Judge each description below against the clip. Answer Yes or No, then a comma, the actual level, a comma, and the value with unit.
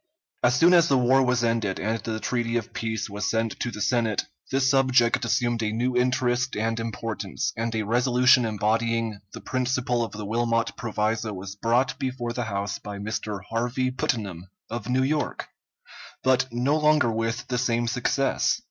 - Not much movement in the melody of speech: Yes, narrow, 2.3 semitones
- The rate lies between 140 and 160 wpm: No, average, 175 wpm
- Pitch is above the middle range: No, low, 115 Hz